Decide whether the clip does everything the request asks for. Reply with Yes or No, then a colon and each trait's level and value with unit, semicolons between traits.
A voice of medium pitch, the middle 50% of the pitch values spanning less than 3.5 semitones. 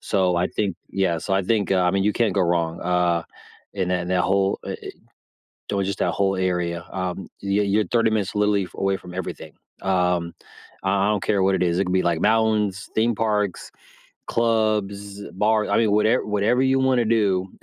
No: very low, 95 Hz; average, 2.7 semitones